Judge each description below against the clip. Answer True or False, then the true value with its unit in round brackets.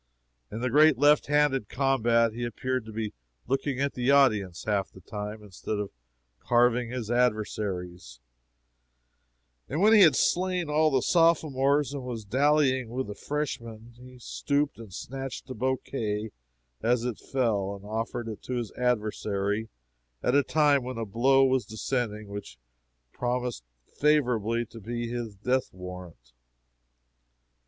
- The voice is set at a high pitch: False (120 Hz)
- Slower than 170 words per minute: True (145 wpm)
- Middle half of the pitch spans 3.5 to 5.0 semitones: True (3.9 semitones)